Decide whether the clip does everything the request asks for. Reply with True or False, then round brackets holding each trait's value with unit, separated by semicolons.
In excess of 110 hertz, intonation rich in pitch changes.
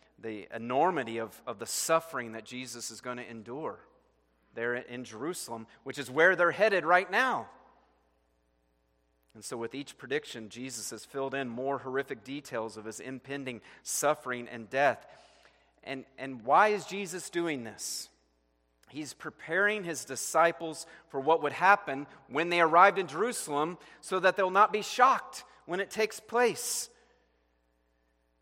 True (135 Hz; 7.0 semitones)